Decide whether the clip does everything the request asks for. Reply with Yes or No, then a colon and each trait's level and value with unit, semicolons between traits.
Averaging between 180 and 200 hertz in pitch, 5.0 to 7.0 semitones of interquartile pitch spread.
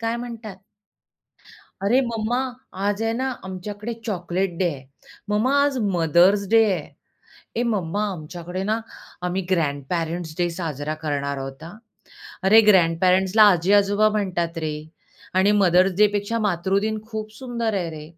No: high, 190 Hz; average, 4.1 semitones